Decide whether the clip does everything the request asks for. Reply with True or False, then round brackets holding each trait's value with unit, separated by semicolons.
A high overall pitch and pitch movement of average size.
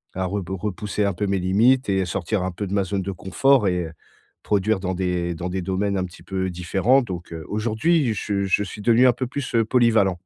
False (100 Hz; 3.1 semitones)